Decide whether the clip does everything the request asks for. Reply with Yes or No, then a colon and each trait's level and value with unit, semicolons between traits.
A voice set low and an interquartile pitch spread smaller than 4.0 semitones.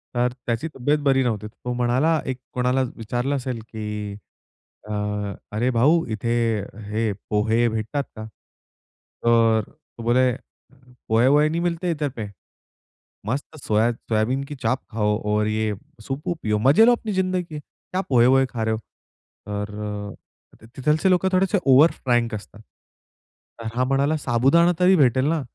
No: low, 125 Hz; average, 5.0 semitones